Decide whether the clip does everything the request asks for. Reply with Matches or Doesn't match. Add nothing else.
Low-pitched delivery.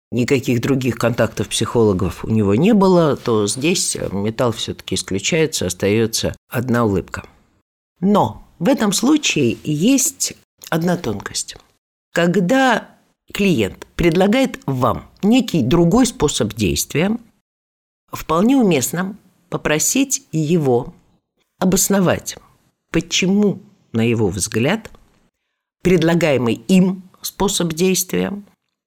Doesn't match